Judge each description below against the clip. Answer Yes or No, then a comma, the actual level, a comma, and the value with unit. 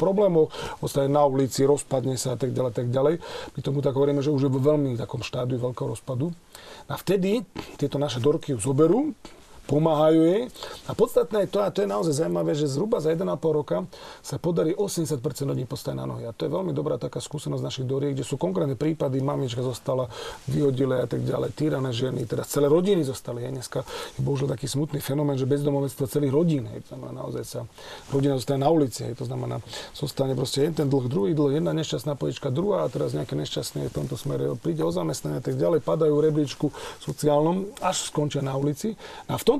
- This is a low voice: No, medium, 145 Hz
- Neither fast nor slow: No, fast, 200 wpm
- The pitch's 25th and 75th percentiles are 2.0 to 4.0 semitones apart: Yes, average, 2.8 semitones